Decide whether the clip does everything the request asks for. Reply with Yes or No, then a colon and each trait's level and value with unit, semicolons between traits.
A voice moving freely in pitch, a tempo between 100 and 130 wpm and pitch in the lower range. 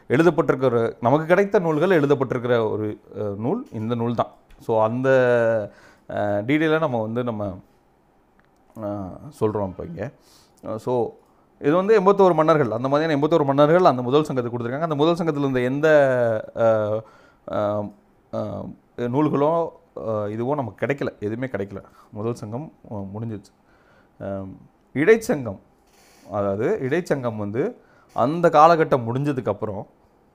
Yes: wide, 5.7 semitones; average, 105 wpm; low, 120 Hz